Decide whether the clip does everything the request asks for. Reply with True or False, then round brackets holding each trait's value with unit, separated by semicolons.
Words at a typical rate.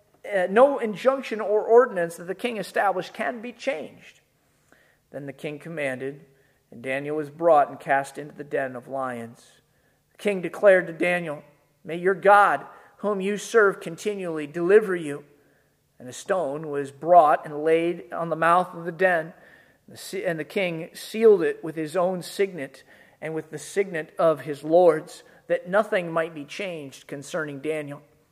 True (165 wpm)